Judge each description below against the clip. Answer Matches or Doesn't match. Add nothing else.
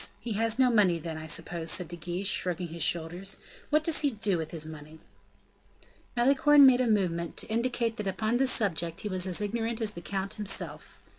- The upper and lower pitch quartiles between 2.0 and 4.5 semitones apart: Doesn't match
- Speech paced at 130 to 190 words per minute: Doesn't match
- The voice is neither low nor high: Doesn't match